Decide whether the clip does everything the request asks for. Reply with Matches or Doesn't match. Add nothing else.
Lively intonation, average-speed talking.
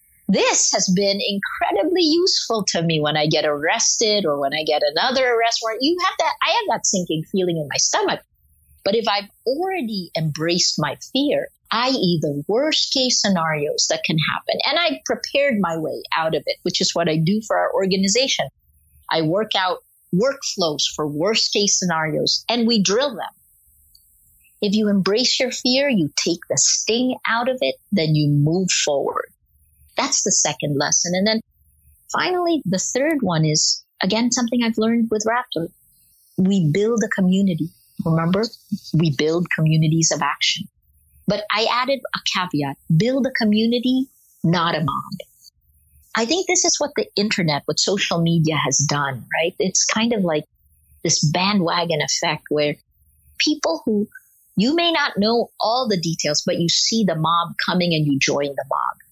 Matches